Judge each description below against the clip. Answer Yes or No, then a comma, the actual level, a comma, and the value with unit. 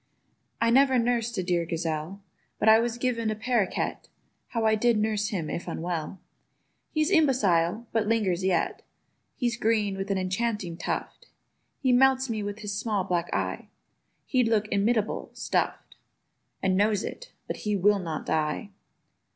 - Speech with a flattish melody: No, average, 4.0 semitones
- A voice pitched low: No, high, 210 Hz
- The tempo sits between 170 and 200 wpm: No, average, 150 wpm